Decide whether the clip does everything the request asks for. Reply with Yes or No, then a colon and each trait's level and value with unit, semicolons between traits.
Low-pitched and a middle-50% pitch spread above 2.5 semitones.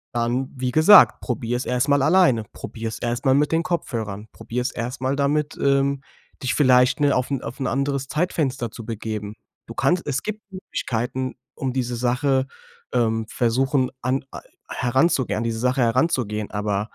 Yes: low, 130 Hz; average, 2.9 semitones